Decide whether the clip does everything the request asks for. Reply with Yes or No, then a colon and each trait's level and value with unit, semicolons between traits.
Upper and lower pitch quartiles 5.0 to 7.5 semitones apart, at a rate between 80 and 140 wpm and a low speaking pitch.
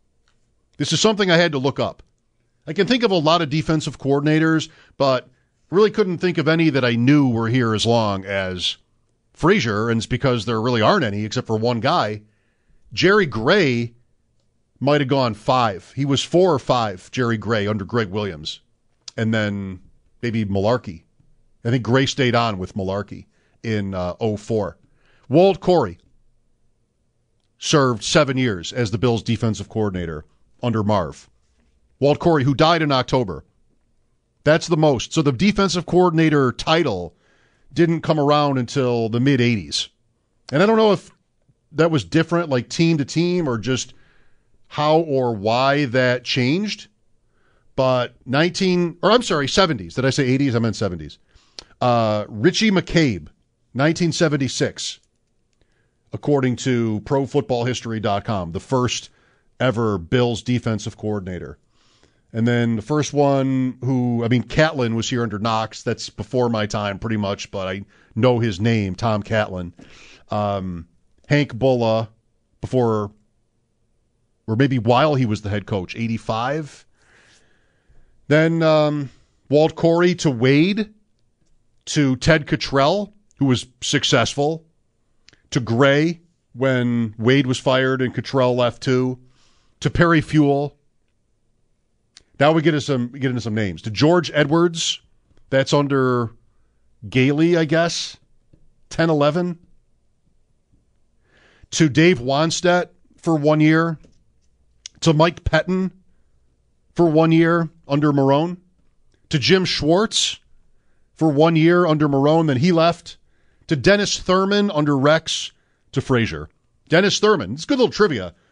Yes: wide, 5.4 semitones; slow, 135 wpm; low, 125 Hz